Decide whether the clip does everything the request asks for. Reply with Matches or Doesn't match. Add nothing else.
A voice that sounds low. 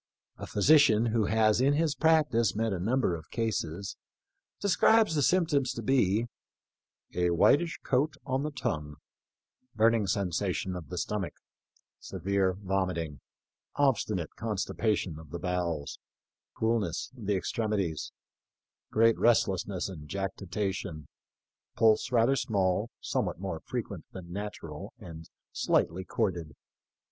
Matches